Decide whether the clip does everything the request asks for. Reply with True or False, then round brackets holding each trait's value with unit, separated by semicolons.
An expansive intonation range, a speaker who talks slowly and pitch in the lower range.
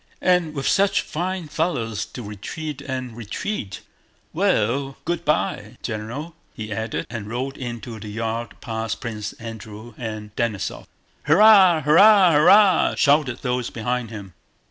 True (5.8 semitones; 130 wpm; 125 Hz)